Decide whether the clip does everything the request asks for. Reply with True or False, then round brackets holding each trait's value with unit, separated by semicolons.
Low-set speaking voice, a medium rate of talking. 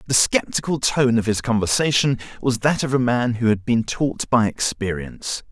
True (125 Hz; 185 wpm)